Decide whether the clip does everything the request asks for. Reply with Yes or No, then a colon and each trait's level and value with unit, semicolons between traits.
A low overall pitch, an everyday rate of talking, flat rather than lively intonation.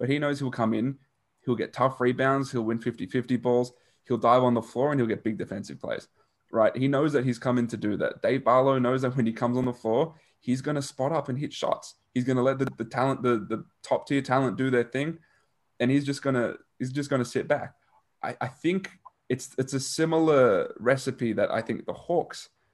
No: low, 130 Hz; fast, 230 wpm; narrow, 2.0 semitones